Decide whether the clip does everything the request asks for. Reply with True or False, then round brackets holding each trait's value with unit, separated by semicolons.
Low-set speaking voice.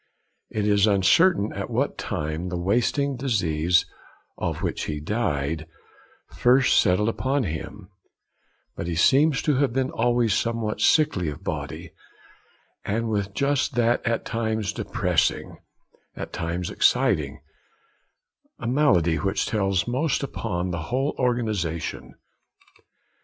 True (105 Hz)